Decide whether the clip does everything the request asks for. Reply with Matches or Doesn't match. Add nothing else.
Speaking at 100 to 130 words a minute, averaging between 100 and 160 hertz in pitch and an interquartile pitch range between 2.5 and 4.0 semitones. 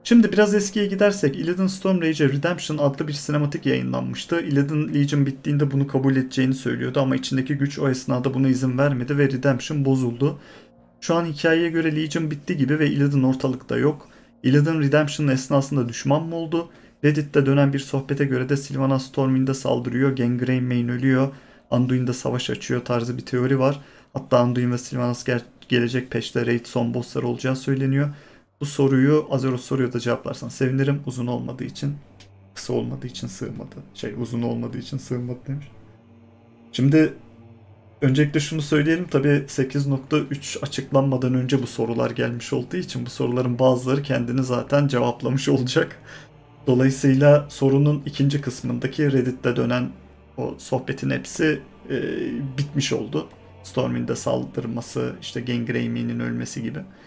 Doesn't match